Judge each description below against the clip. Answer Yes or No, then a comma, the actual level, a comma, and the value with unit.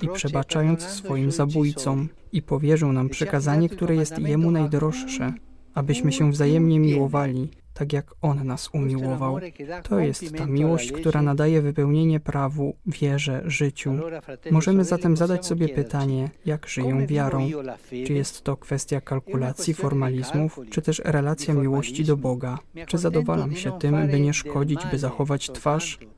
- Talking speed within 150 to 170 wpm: No, average, 140 wpm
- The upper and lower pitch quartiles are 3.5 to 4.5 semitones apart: No, narrow, 2.5 semitones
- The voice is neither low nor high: Yes, medium, 145 Hz